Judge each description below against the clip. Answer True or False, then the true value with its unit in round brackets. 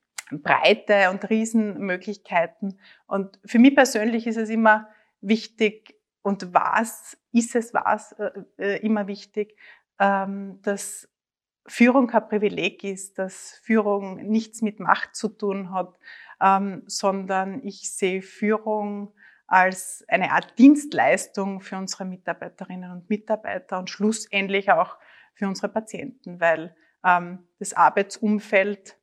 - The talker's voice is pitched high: True (205 Hz)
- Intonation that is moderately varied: False (2.1 semitones)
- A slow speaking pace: True (120 wpm)